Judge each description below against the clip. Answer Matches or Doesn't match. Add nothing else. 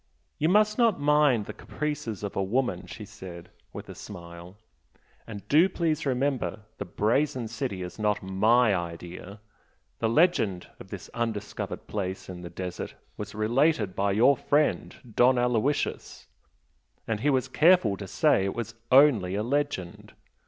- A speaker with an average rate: Matches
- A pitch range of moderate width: Doesn't match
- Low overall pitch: Matches